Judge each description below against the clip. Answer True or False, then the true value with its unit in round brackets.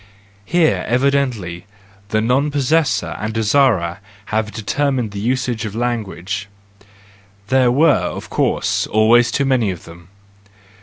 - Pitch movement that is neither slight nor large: True (4.5 semitones)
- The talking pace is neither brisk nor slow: False (115 wpm)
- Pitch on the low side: True (110 Hz)